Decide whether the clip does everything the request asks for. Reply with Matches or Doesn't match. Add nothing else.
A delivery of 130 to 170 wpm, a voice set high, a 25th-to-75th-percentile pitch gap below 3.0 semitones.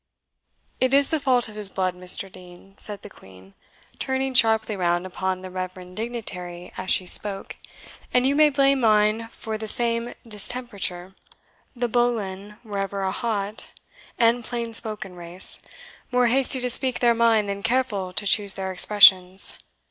Doesn't match